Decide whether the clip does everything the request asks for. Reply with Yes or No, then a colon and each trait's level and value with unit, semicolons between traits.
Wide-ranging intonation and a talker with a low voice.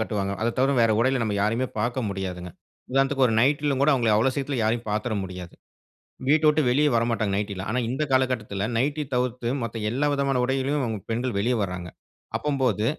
No: average, 4.0 semitones; low, 120 Hz